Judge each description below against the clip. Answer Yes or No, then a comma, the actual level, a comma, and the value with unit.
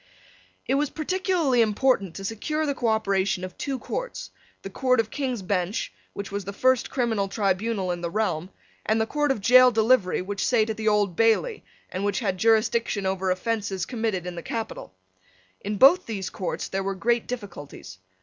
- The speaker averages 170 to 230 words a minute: Yes, average, 180 wpm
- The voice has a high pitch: Yes, high, 215 Hz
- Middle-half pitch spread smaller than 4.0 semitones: No, average, 4.3 semitones